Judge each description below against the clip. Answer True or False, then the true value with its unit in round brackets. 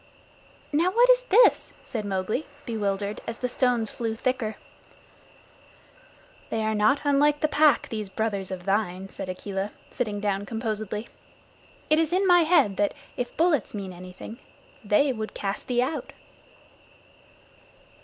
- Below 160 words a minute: True (140 wpm)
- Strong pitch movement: True (6.0 semitones)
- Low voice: False (220 Hz)